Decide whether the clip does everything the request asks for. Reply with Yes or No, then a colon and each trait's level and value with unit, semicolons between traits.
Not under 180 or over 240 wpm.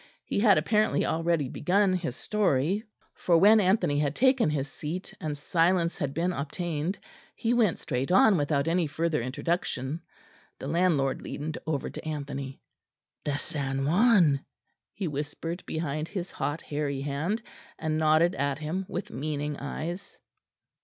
No: average, 145 wpm